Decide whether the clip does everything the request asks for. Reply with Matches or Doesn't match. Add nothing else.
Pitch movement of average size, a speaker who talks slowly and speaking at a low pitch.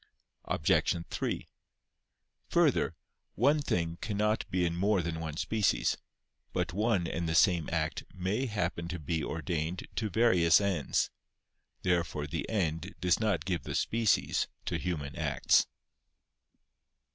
Matches